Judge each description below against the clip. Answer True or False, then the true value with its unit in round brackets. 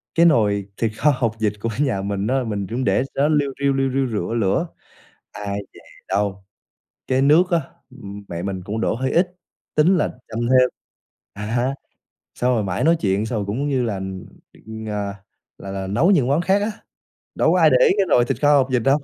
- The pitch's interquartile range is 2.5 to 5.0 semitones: False (5.6 semitones)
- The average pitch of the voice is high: False (120 Hz)